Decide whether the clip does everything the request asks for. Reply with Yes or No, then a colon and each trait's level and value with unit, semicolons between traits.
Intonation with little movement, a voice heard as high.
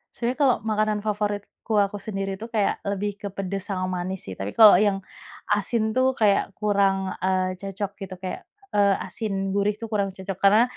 Yes: narrow, 1.7 semitones; high, 200 Hz